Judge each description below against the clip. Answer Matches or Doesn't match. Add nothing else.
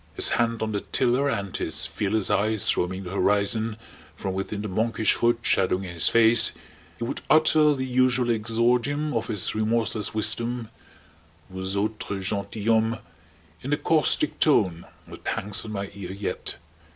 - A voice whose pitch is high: Doesn't match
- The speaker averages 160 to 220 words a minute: Doesn't match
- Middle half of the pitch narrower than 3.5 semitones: Matches